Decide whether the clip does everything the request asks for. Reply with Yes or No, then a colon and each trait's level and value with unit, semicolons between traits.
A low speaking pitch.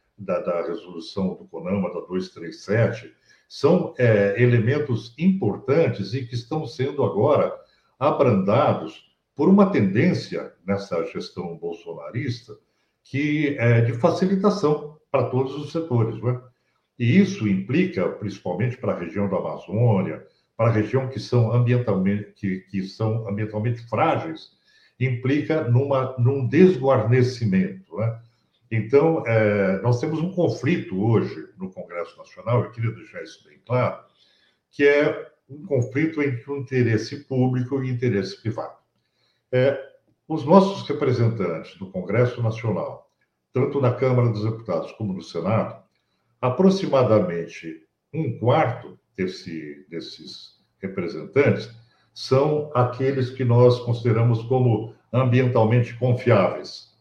Yes: low, 125 Hz